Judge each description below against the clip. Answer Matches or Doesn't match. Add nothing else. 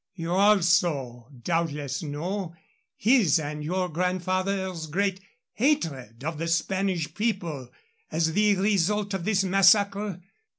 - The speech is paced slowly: Matches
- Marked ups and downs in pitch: Doesn't match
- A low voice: Doesn't match